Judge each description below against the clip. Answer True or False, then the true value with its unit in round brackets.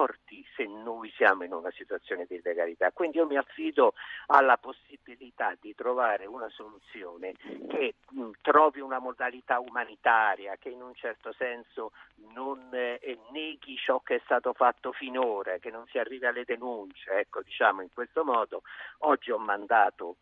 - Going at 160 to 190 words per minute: False (150 wpm)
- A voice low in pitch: False (270 Hz)